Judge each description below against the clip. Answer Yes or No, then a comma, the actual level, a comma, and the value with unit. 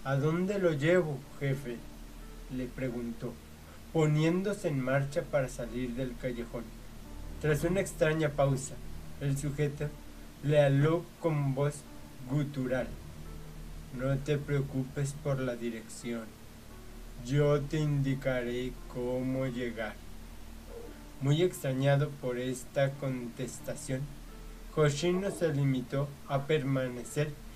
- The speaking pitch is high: No, low, 130 Hz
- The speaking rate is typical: No, slow, 100 wpm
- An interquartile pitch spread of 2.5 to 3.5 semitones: No, average, 3.9 semitones